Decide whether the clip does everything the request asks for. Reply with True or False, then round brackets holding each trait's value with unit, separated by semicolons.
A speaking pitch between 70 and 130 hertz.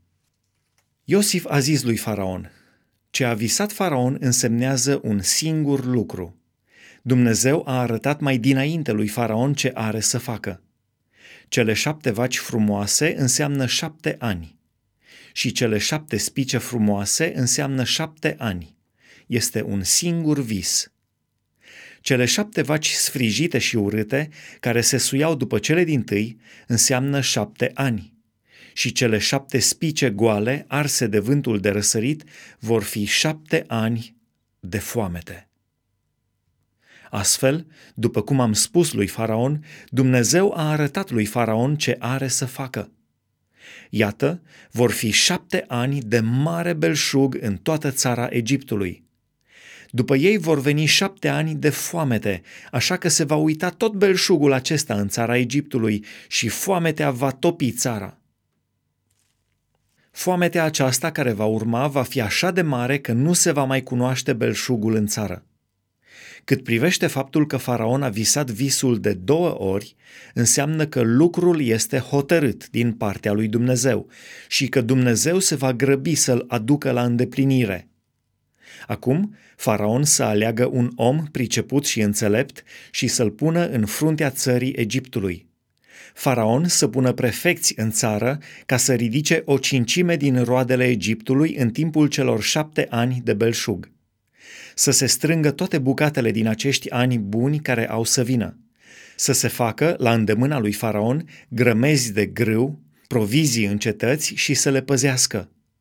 True (125 Hz)